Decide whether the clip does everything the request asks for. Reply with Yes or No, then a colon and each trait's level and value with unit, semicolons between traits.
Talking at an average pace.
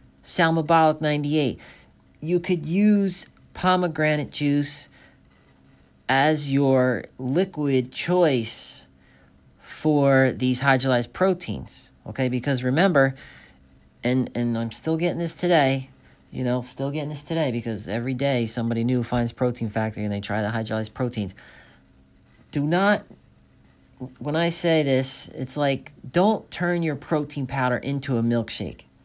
No: slow, 125 wpm